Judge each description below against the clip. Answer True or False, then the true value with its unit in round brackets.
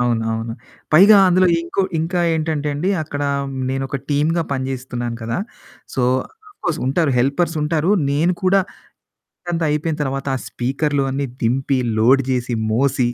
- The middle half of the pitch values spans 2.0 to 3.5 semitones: False (4.1 semitones)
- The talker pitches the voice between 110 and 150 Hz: True (140 Hz)